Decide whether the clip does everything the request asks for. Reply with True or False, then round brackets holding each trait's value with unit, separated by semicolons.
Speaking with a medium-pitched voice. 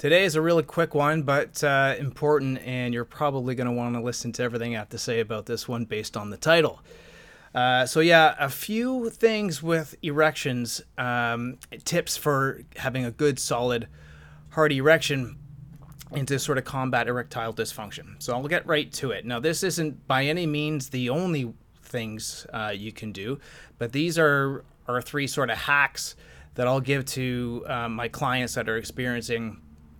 False (130 Hz)